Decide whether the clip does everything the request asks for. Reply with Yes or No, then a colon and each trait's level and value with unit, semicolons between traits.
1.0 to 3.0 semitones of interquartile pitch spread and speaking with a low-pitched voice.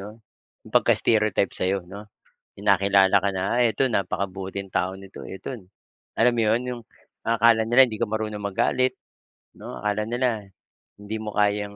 Yes: narrow, 2.6 semitones; low, 105 Hz